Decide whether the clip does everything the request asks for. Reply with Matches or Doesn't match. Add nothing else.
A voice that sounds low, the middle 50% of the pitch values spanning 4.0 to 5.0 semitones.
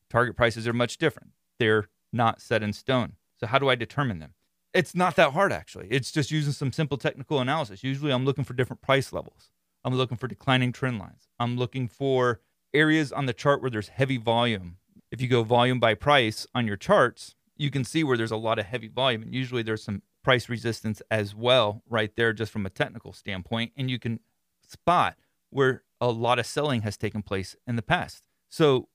Doesn't match